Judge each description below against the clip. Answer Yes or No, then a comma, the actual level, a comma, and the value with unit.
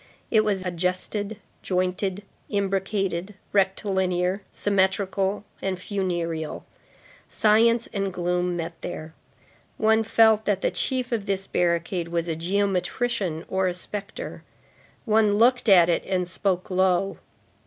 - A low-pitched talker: No, high, 190 Hz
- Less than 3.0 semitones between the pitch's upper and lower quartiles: Yes, narrow, 2.5 semitones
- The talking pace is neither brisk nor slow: No, slow, 120 wpm